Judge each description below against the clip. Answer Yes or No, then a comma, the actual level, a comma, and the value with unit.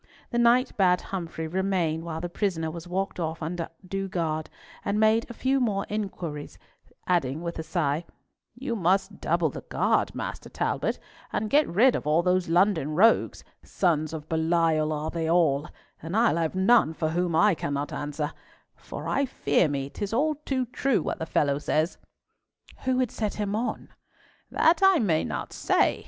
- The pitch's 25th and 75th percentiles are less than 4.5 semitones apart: No, average, 4.9 semitones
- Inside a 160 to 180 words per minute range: Yes, average, 170 wpm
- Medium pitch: Yes, medium, 175 Hz